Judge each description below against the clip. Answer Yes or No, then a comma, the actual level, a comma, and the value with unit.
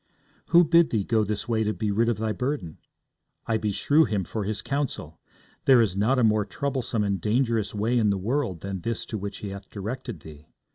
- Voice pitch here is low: Yes, low, 110 Hz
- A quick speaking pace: Yes, fast, 220 wpm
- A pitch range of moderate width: Yes, average, 3.7 semitones